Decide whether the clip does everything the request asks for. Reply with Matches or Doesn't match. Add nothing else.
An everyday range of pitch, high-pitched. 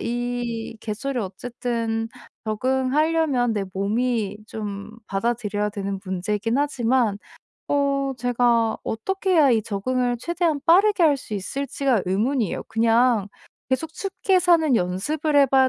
Matches